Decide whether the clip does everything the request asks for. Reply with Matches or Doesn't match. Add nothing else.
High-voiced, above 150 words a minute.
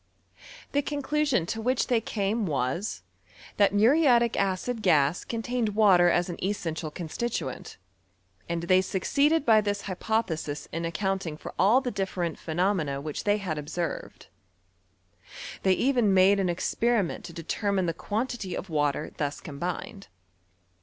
Doesn't match